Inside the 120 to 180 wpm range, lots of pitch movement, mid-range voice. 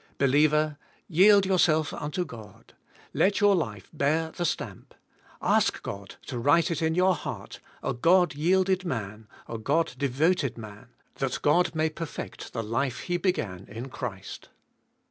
Yes: average, 150 wpm; wide, 6.7 semitones; medium, 150 Hz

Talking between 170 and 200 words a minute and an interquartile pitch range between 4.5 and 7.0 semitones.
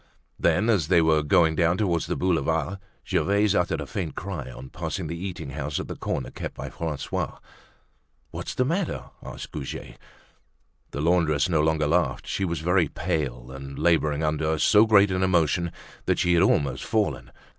No: average, 175 wpm; average, 3.6 semitones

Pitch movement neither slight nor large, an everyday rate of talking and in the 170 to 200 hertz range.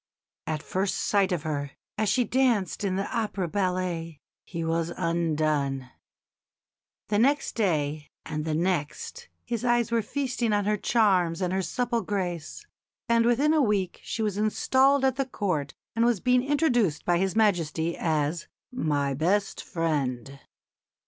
No: wide, 6.4 semitones; average, 150 wpm; high, 190 Hz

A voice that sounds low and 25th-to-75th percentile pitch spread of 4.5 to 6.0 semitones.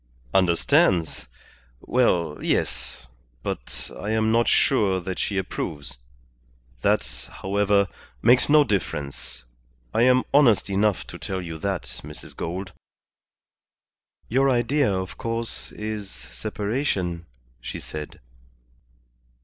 Yes: low, 100 Hz; average, 4.9 semitones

